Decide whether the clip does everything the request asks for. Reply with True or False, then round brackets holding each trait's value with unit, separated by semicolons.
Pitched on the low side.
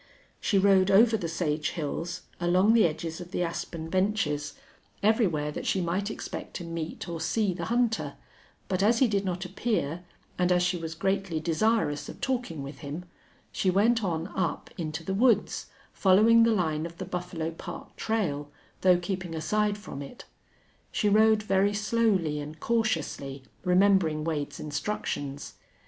False (180 Hz)